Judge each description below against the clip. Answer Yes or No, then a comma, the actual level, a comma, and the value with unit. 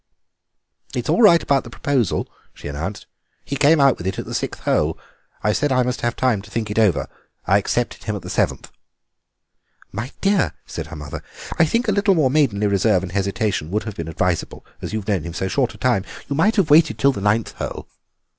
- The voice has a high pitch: No, low, 110 Hz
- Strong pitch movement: Yes, wide, 6.3 semitones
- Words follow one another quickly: Yes, fast, 220 wpm